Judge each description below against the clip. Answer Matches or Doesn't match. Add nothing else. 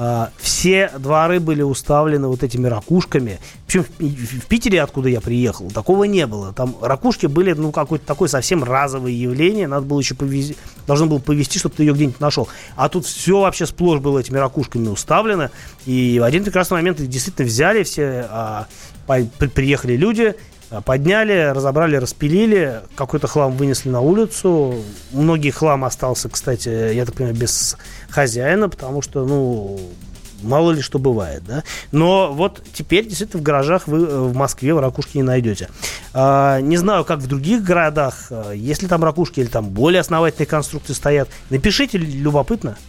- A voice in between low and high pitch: Matches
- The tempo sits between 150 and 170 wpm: Matches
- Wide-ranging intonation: Doesn't match